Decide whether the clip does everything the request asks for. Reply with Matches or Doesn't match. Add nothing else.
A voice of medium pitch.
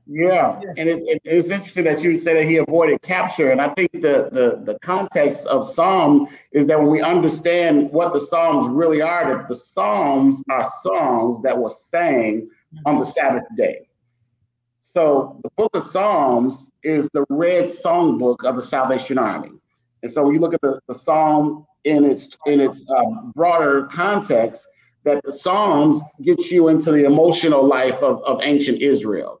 Matches